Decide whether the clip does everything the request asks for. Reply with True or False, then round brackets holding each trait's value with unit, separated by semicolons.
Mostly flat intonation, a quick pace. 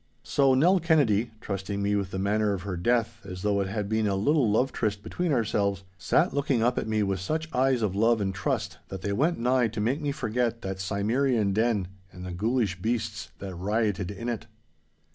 False (3.7 semitones; 210 wpm)